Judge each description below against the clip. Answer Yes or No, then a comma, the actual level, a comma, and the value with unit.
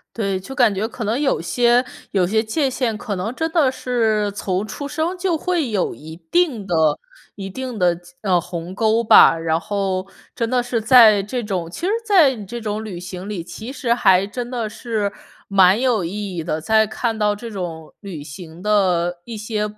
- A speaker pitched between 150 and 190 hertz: No, high, 210 Hz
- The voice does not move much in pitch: No, average, 4.4 semitones